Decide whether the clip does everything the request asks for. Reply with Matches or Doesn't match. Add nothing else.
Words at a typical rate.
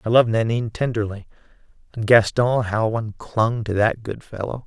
Matches